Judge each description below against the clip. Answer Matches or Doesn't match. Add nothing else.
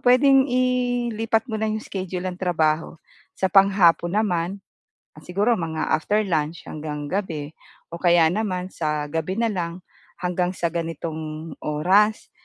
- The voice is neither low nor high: Matches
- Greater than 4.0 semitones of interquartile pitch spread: Matches